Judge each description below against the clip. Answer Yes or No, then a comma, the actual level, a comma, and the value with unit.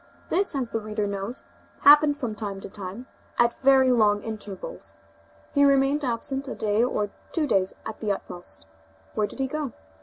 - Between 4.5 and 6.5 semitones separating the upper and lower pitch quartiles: Yes, average, 4.9 semitones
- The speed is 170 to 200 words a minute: Yes, average, 175 wpm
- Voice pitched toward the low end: No, high, 230 Hz